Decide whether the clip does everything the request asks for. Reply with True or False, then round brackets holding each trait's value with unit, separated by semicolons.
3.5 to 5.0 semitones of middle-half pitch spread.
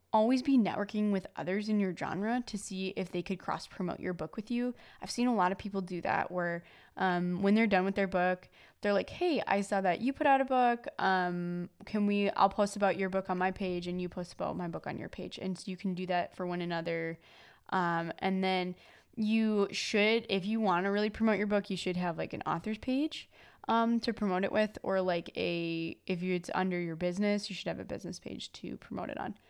False (2.9 semitones)